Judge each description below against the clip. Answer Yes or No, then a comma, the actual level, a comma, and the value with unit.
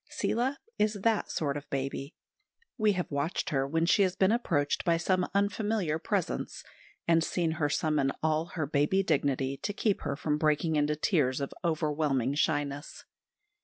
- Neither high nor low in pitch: Yes, medium, 155 Hz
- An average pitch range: Yes, average, 4.5 semitones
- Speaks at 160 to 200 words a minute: Yes, average, 165 wpm